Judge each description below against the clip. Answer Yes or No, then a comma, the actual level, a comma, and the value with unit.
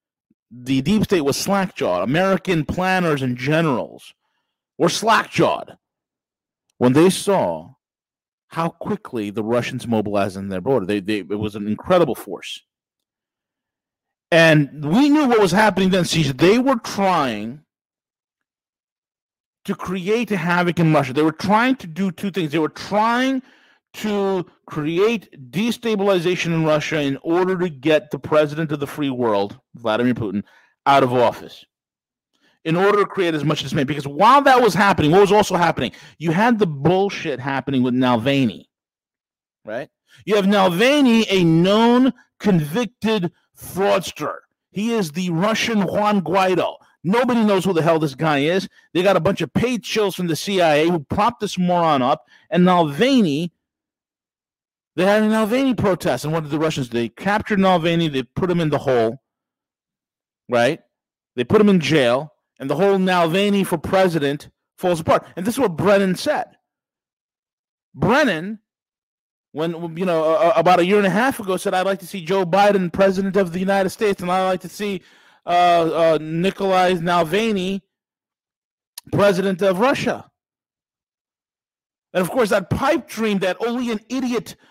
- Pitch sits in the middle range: Yes, medium, 180 Hz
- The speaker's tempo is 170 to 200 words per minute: No, average, 160 wpm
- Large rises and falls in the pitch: No, average, 4.7 semitones